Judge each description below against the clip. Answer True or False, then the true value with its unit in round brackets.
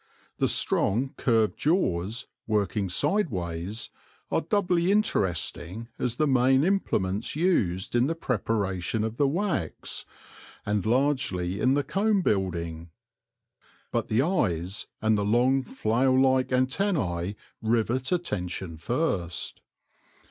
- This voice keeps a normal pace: False (115 wpm)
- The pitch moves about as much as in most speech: False (6.7 semitones)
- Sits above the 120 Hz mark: False (115 Hz)